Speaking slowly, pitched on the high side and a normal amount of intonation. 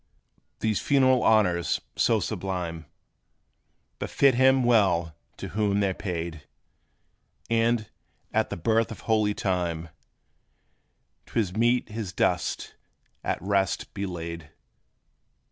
No: slow, 110 wpm; low, 100 Hz; average, 4.7 semitones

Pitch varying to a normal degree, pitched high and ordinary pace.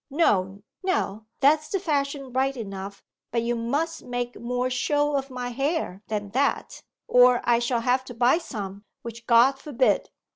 Yes: average, 3.3 semitones; very high, 250 Hz; average, 160 wpm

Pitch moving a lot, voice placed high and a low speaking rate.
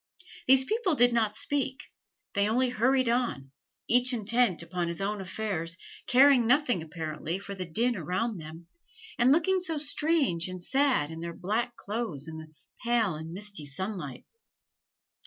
No: wide, 6.8 semitones; high, 215 Hz; average, 155 wpm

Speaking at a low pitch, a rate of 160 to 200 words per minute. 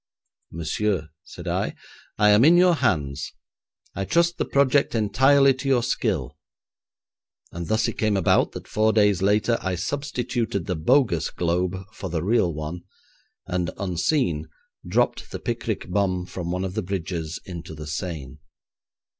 No: very low, 95 Hz; average, 150 wpm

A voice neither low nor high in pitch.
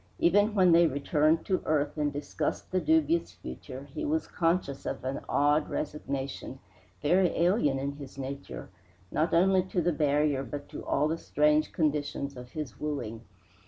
Yes: medium, 150 Hz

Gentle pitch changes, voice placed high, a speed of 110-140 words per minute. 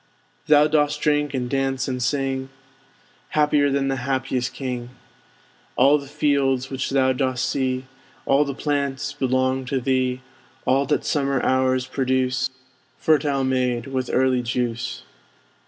No: narrow, 1.5 semitones; low, 130 Hz; slow, 135 wpm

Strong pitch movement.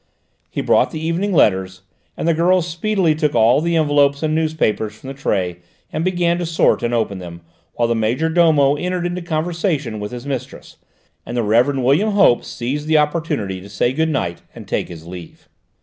Yes: wide, 6.7 semitones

